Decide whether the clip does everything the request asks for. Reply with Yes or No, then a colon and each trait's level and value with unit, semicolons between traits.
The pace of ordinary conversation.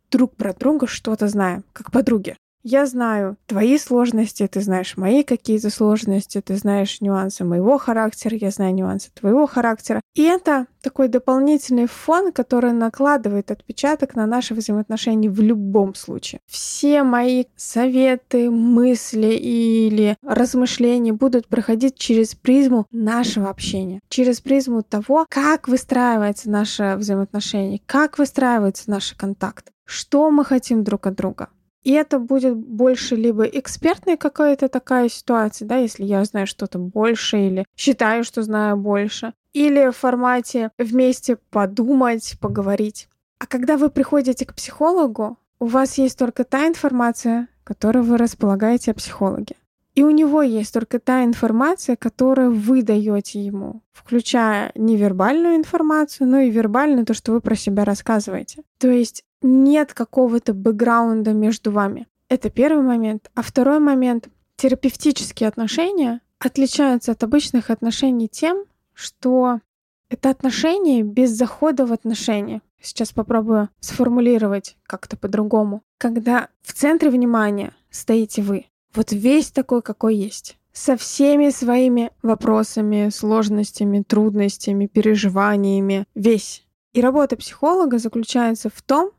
Yes: average, 130 wpm